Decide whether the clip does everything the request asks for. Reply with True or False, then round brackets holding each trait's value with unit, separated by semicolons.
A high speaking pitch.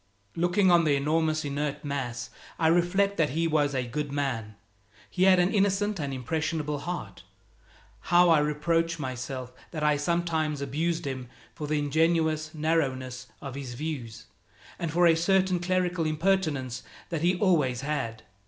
False (155 Hz)